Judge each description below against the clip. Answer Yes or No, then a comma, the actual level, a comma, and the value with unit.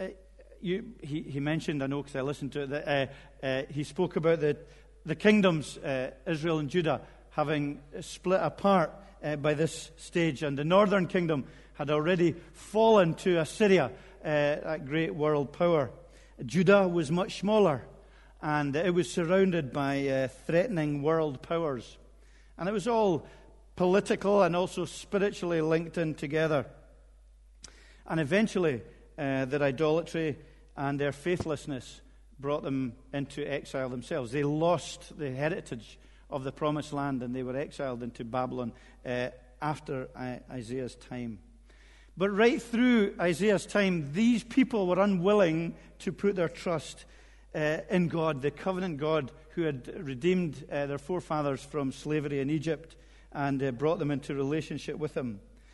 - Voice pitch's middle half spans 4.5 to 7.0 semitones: No, average, 4.1 semitones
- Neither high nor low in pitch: Yes, medium, 155 Hz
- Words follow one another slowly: No, average, 150 wpm